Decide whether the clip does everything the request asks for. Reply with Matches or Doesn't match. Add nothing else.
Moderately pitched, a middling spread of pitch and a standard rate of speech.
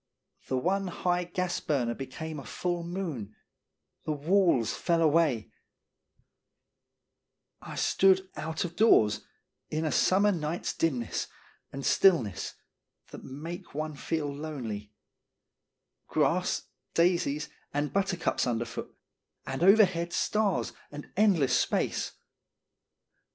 Doesn't match